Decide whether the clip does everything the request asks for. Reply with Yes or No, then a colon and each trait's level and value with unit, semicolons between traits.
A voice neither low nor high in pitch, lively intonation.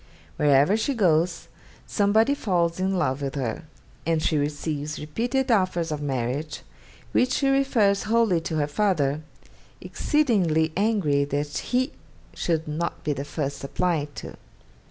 Yes: medium, 165 Hz; wide, 6.0 semitones